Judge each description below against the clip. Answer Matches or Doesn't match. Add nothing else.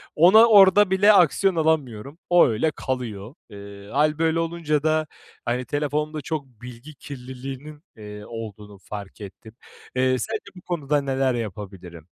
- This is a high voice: Doesn't match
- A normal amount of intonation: Doesn't match